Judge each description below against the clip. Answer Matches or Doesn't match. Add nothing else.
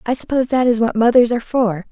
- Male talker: Doesn't match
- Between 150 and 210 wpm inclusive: Doesn't match